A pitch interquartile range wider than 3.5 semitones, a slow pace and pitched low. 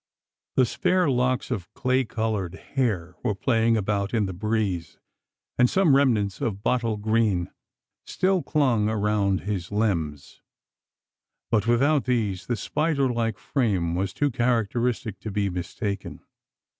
Yes: average, 4.1 semitones; slow, 130 wpm; low, 110 Hz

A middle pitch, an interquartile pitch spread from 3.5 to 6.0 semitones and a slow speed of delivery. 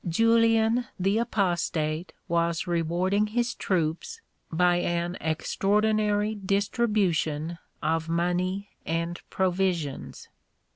Yes: medium, 180 Hz; average, 3.9 semitones; slow, 85 wpm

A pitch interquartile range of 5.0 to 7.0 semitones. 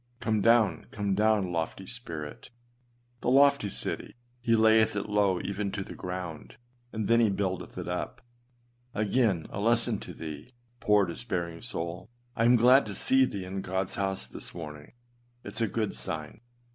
No: average, 3.8 semitones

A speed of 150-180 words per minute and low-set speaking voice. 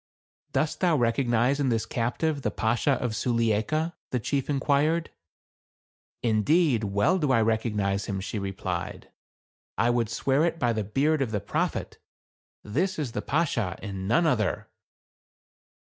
Yes: average, 165 wpm; low, 120 Hz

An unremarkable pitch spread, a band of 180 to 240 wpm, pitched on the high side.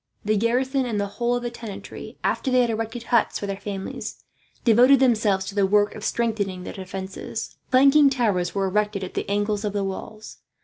Yes: average, 3.3 semitones; average, 195 wpm; high, 210 Hz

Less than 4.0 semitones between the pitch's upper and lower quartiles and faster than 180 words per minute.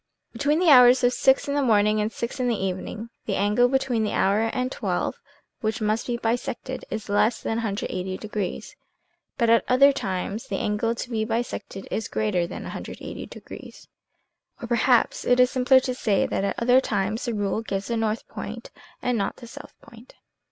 Yes: average, 3.1 semitones; average, 195 wpm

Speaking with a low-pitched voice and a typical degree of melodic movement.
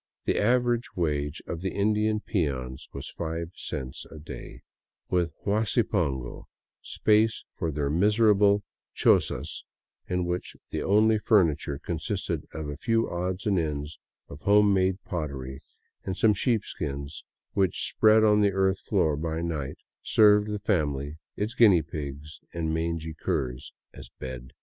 No: very low, 85 Hz; wide, 5.8 semitones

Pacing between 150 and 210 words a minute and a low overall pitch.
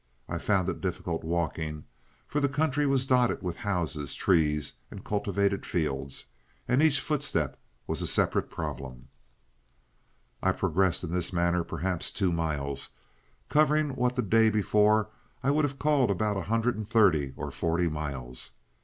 Yes: average, 155 wpm; very low, 95 Hz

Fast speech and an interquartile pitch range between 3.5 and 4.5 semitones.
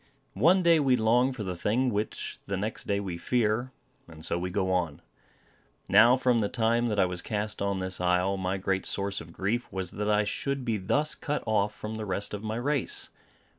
Yes: fast, 210 wpm; average, 4.1 semitones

